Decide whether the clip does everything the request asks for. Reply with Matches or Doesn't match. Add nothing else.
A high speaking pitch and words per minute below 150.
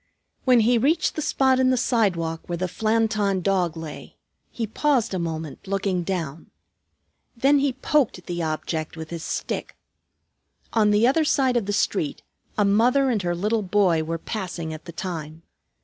Doesn't match